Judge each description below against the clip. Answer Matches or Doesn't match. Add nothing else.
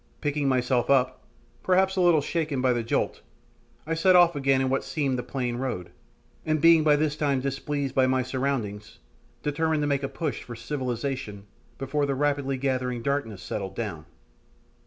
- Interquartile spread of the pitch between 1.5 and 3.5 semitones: Matches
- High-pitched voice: Doesn't match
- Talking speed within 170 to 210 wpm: Matches